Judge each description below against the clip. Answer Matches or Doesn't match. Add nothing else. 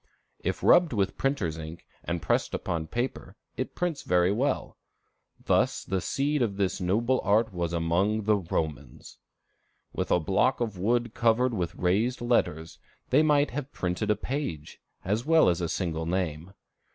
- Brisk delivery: Doesn't match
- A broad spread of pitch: Matches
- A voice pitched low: Matches